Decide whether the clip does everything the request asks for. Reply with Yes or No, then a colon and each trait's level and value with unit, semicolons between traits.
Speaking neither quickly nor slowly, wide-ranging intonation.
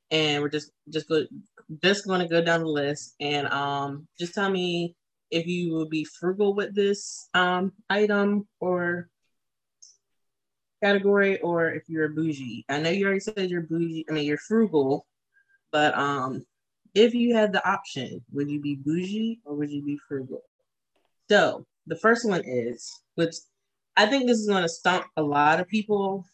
No: average, 170 wpm; average, 5.0 semitones